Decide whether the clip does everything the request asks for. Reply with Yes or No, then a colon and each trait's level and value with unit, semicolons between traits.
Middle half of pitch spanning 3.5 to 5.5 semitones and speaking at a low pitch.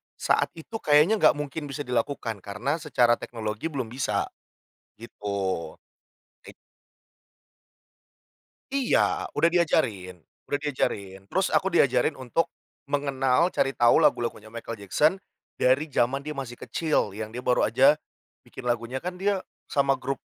Yes: average, 4.6 semitones; low, 130 Hz